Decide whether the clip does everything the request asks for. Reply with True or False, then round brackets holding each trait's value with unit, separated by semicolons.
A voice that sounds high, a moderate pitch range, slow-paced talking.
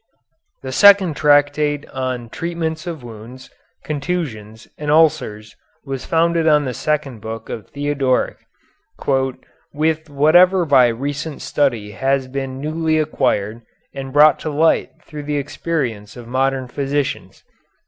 False (145 Hz; 3.4 semitones; 130 wpm)